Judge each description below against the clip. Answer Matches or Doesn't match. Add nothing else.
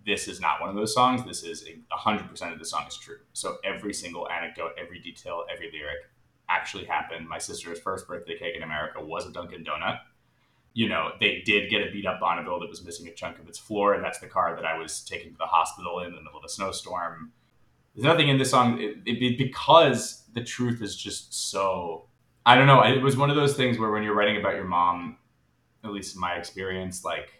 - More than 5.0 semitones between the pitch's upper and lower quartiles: Matches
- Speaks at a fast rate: Matches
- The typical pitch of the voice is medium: Doesn't match